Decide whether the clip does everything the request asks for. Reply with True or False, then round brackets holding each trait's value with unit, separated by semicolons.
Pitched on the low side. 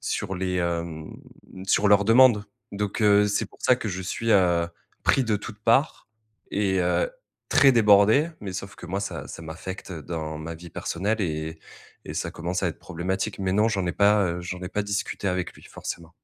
True (95 Hz)